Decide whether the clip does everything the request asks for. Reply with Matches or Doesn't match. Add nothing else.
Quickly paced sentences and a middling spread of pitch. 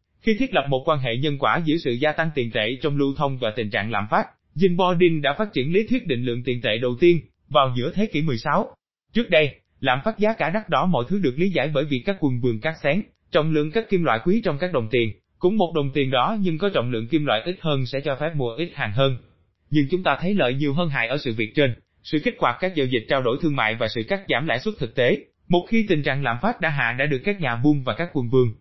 Doesn't match